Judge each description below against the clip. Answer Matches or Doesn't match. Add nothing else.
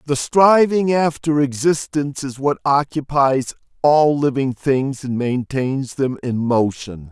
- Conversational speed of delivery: Doesn't match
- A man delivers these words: Matches